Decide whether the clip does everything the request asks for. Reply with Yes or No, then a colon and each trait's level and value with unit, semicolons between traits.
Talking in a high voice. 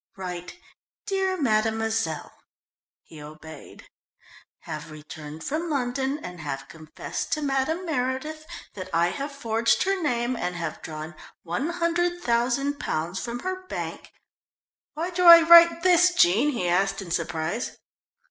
Yes: high, 240 Hz